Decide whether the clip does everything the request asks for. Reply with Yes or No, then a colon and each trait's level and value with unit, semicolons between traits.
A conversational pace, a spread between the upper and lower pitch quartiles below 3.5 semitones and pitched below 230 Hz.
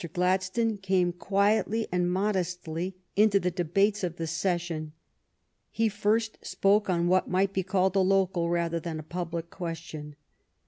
Yes: average, 145 wpm; narrow, 2.5 semitones; medium, 185 Hz